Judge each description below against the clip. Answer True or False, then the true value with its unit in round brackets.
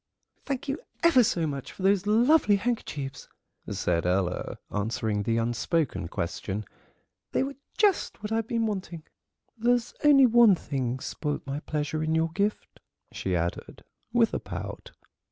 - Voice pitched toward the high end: False (165 Hz)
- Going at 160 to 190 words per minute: False (145 wpm)